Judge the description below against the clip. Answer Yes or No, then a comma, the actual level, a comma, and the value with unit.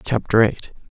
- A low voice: Yes, low, 110 Hz